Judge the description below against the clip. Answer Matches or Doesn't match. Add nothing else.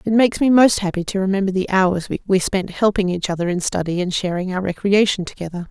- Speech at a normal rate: Doesn't match